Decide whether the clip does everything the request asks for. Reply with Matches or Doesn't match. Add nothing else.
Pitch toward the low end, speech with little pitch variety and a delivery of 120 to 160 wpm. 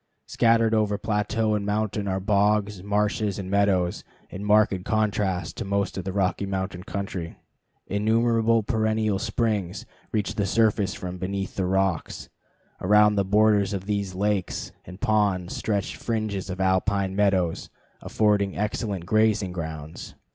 Matches